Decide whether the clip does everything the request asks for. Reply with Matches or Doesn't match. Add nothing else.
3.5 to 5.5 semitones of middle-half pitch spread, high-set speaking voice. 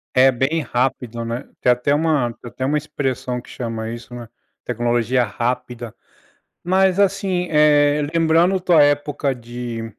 Doesn't match